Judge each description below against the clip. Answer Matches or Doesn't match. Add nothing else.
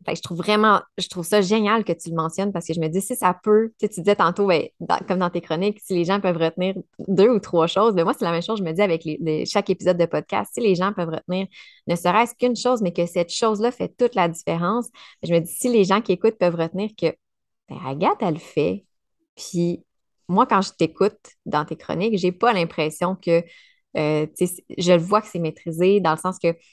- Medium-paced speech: Doesn't match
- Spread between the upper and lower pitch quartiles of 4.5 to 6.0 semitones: Doesn't match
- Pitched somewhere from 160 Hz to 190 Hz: Matches